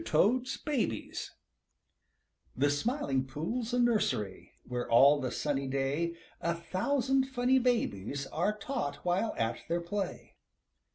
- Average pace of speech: No, slow, 120 wpm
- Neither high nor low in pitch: Yes, medium, 170 Hz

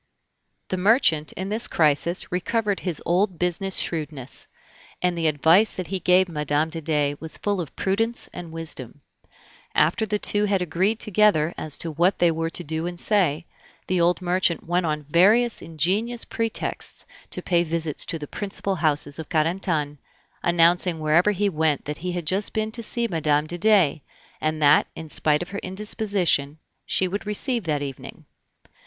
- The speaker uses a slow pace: No, average, 175 wpm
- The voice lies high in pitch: No, medium, 175 Hz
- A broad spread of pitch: No, average, 4.0 semitones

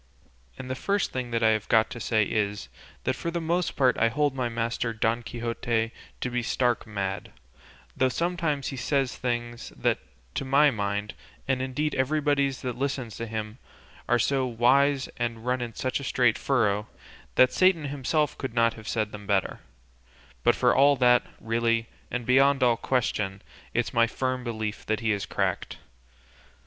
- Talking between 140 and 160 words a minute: No, average, 170 wpm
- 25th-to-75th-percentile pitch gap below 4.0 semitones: Yes, average, 3.0 semitones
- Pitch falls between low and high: No, low, 120 Hz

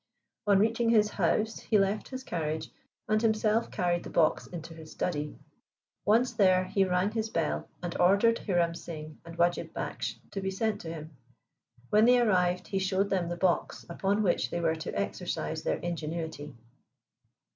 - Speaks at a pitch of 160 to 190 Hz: Yes, medium, 185 Hz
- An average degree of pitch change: Yes, average, 4.0 semitones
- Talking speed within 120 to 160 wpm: No, average, 170 wpm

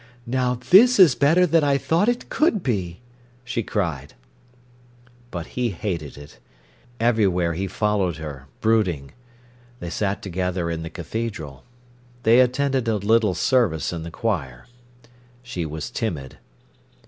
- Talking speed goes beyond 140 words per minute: No, slow, 135 wpm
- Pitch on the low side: Yes, low, 105 Hz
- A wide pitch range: Yes, wide, 7.0 semitones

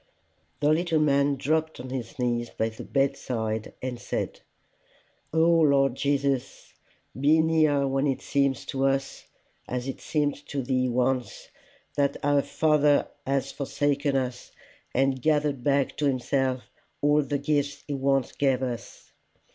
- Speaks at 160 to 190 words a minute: No, average, 140 wpm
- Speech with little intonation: Yes, narrow, 1.9 semitones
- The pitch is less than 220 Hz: Yes, medium, 140 Hz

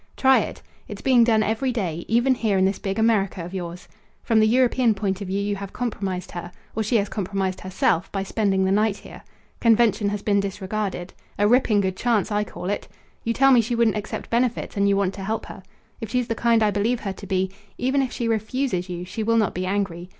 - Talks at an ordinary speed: No, fast, 230 wpm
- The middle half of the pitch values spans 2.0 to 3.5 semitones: Yes, average, 3.1 semitones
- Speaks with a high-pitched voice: Yes, high, 205 Hz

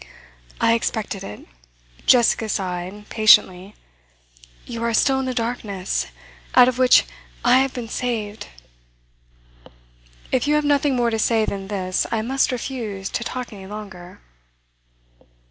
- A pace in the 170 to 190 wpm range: No, slow, 135 wpm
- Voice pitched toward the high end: Yes, high, 225 Hz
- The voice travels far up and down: No, average, 3.8 semitones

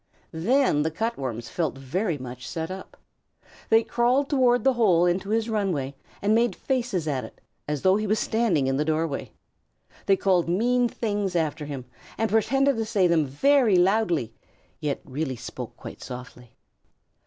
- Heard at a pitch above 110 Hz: Yes, medium, 185 Hz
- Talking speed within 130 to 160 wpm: No, average, 170 wpm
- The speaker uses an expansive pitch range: Yes, wide, 7.2 semitones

